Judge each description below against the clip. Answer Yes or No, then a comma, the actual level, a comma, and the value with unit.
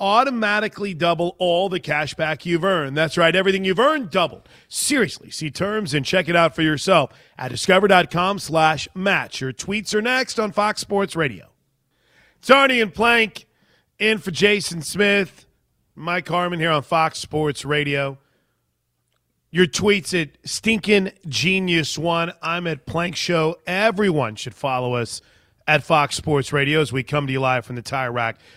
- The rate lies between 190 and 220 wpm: No, average, 165 wpm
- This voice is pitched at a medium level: Yes, medium, 170 Hz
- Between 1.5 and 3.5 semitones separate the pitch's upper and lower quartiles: No, average, 5.0 semitones